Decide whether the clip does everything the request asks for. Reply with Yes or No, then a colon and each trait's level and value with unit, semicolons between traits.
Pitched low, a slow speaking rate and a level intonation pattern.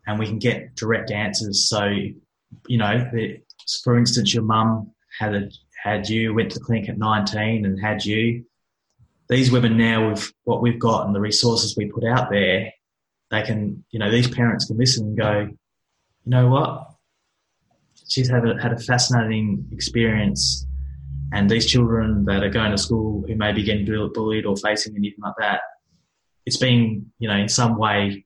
No: low, 110 Hz; average, 180 wpm; narrow, 2.1 semitones